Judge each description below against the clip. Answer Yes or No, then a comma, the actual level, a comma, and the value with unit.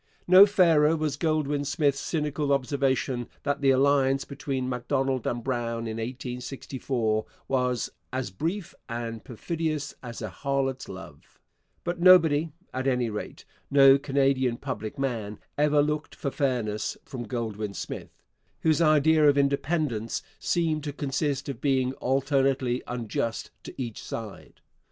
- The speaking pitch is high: No, low, 135 Hz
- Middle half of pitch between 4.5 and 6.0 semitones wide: No, average, 3.3 semitones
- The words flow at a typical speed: No, slow, 130 wpm